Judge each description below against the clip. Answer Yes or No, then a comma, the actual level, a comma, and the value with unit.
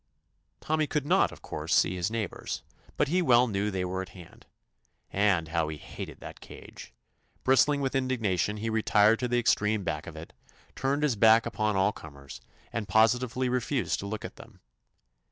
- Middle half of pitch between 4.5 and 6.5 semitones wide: Yes, average, 5.0 semitones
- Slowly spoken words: No, average, 190 wpm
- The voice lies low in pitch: Yes, low, 110 Hz